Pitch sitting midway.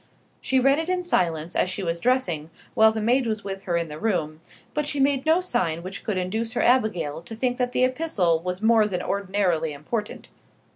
No: high, 210 Hz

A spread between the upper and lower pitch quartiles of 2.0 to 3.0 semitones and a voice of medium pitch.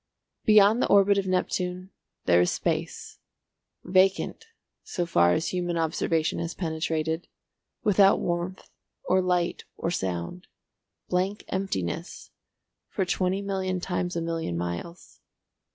Yes: average, 2.7 semitones; medium, 180 Hz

